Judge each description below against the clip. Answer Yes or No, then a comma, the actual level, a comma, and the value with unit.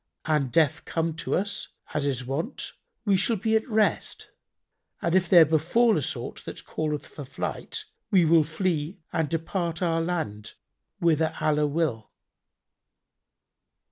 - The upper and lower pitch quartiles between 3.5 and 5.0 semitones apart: No, average, 3.0 semitones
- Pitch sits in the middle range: Yes, medium, 165 Hz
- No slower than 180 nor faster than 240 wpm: No, average, 140 wpm